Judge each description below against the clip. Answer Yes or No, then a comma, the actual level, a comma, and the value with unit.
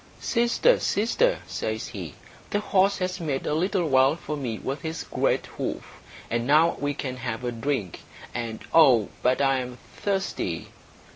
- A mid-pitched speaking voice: Yes, medium, 145 Hz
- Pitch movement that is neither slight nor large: No, wide, 6.7 semitones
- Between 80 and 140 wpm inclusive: No, average, 160 wpm